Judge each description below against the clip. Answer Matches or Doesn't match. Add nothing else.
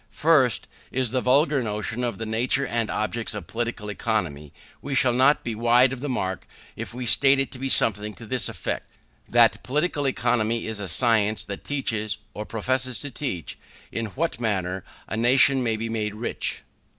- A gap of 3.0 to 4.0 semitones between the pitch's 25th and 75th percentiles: Matches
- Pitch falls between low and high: Doesn't match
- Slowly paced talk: Doesn't match